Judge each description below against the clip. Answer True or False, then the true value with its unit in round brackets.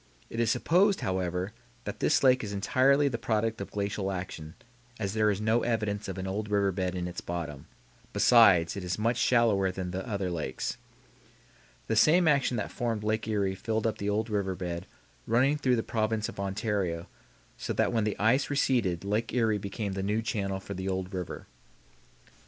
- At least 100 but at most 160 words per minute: False (190 wpm)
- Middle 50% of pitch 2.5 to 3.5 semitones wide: True (3.2 semitones)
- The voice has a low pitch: True (105 Hz)